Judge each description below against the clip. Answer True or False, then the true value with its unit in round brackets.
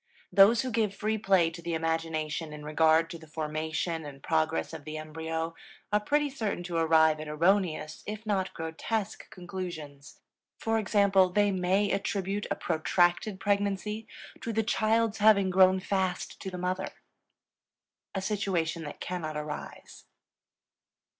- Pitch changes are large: False (4.1 semitones)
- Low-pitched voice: False (180 Hz)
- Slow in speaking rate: False (145 wpm)